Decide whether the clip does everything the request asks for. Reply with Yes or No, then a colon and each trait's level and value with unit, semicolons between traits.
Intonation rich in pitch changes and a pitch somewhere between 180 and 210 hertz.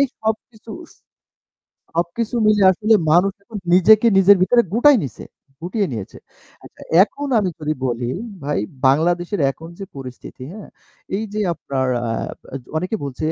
Yes: wide, 6.5 semitones; medium, 185 Hz